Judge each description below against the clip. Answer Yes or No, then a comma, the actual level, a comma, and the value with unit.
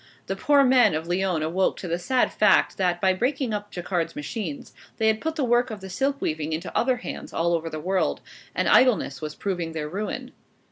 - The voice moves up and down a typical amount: No, wide, 6.5 semitones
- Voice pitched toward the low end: No, high, 190 Hz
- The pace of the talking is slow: No, fast, 205 wpm